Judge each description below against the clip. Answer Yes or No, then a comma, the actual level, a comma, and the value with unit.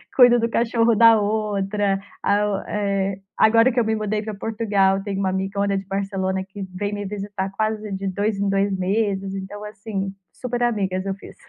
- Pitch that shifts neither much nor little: No, narrow, 1.9 semitones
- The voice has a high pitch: Yes, high, 200 Hz